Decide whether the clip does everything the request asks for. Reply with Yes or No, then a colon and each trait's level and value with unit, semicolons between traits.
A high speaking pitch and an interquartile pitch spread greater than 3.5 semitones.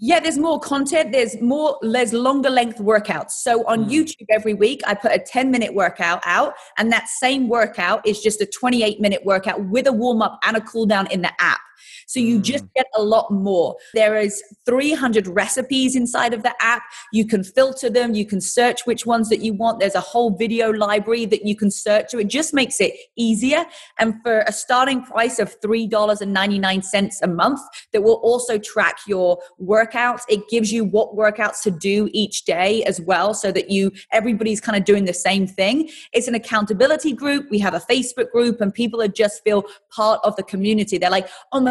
No: high, 220 Hz; average, 2.9 semitones